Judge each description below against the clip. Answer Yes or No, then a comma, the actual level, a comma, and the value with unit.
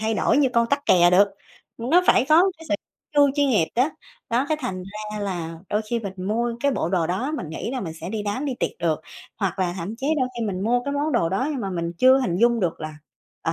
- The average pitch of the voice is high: Yes, high, 220 Hz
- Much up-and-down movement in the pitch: Yes, wide, 6.1 semitones